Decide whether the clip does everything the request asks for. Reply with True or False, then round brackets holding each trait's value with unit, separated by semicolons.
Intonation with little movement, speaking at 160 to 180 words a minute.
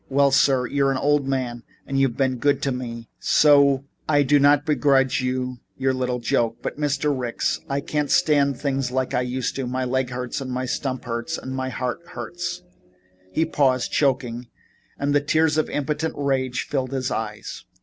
False (2.1 semitones; 190 wpm)